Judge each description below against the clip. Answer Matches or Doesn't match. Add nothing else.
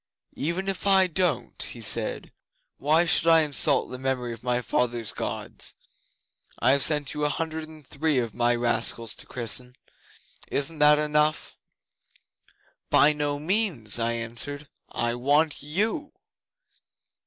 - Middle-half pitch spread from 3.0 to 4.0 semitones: Doesn't match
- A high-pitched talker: Doesn't match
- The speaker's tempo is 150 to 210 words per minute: Doesn't match